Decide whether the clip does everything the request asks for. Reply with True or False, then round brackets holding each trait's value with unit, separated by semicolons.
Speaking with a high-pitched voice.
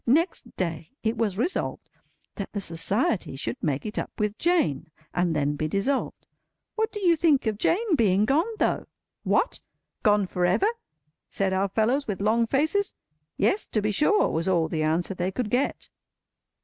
True (210 Hz)